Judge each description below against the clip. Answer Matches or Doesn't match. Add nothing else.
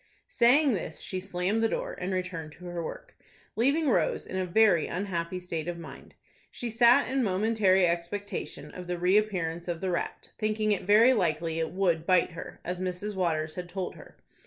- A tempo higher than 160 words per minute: Matches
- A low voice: Doesn't match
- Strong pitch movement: Doesn't match